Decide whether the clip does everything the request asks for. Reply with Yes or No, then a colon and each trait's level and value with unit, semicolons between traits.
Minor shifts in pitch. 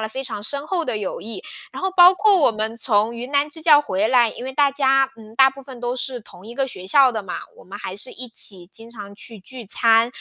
No: average, 3.9 semitones